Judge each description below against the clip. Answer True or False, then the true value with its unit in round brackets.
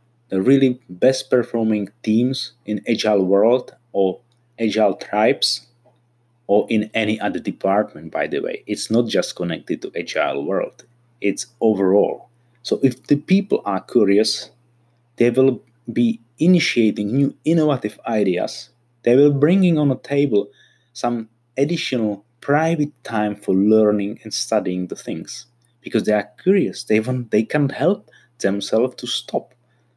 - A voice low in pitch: True (120 Hz)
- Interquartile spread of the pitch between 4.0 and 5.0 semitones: False (3.3 semitones)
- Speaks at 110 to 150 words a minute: True (140 wpm)